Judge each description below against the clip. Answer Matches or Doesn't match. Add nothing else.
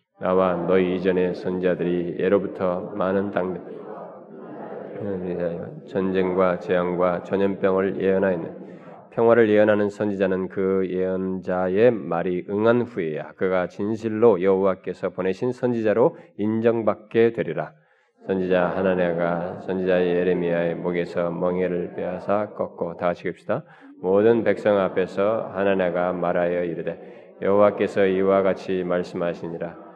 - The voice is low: Matches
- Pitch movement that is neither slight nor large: Doesn't match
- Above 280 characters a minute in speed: Matches